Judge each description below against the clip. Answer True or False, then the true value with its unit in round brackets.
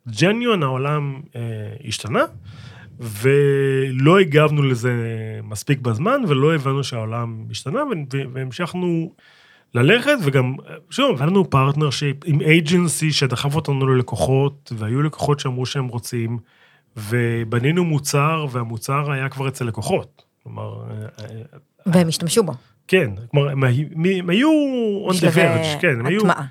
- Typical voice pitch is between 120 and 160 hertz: True (140 Hz)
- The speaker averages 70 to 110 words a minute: True (105 wpm)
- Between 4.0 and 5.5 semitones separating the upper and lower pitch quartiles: True (4.9 semitones)